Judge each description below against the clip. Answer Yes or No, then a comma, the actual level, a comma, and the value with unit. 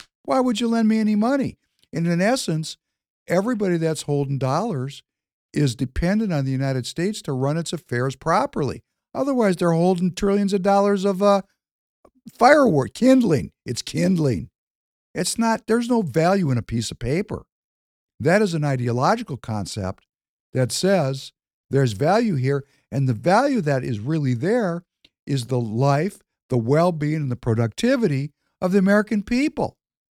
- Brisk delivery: No, average, 150 wpm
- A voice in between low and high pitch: Yes, medium, 165 Hz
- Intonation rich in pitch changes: Yes, wide, 7.2 semitones